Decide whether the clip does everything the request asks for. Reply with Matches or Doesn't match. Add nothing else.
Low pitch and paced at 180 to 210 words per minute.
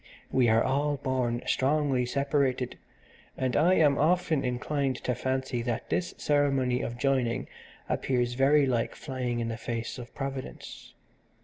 Doesn't match